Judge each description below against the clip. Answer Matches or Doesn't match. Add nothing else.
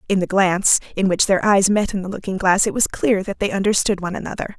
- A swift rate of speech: Matches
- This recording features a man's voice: Doesn't match